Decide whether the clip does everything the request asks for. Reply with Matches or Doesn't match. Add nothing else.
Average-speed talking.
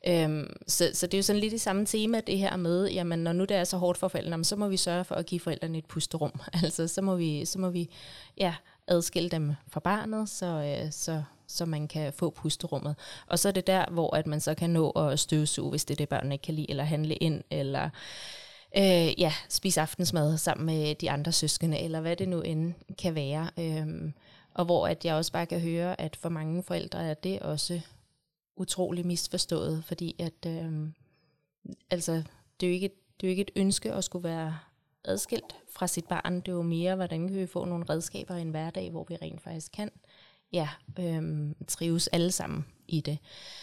Matches